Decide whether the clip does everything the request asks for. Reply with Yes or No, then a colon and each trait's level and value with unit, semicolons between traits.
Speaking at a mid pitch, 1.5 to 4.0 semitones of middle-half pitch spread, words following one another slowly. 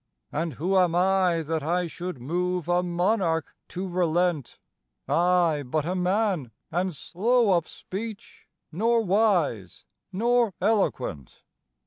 Yes: medium, 180 Hz; average, 2.9 semitones; slow, 120 wpm